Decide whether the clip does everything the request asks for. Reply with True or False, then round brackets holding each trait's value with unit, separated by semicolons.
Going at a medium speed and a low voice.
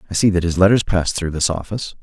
False (265 wpm; 90 Hz)